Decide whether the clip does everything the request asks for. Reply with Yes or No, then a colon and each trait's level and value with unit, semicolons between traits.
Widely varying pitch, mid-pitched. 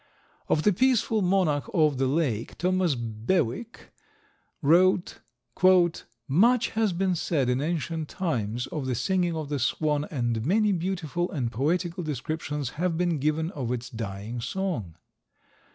Yes: wide, 6.1 semitones; medium, 155 Hz